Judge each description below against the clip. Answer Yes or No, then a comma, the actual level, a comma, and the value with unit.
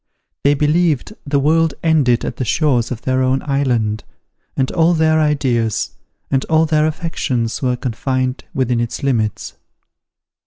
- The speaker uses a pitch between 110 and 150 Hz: Yes, low, 135 Hz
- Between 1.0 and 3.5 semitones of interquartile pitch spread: No, average, 4.0 semitones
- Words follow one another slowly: No, average, 145 wpm